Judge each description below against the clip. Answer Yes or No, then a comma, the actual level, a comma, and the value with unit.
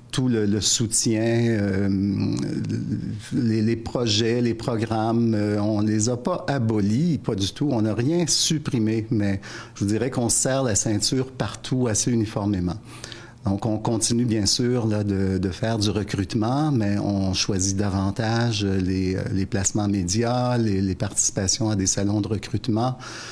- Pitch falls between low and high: No, low, 110 Hz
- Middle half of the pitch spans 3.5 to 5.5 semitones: No, average, 2.7 semitones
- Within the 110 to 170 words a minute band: Yes, average, 155 wpm